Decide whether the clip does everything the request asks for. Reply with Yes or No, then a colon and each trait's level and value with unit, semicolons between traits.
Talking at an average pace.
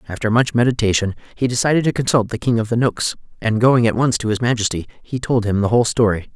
No: fast, 235 wpm